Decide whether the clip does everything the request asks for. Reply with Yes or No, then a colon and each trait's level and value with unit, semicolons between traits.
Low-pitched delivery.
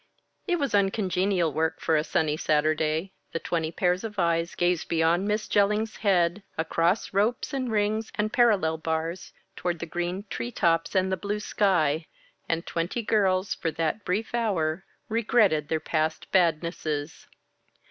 No: medium, 180 Hz